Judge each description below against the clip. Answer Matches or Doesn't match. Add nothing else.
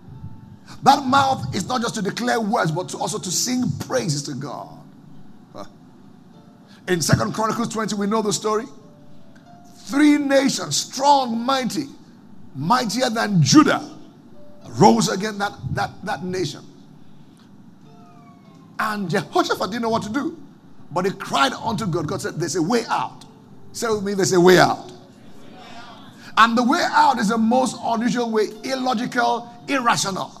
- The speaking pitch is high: Matches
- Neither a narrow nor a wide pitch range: Matches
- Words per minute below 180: Matches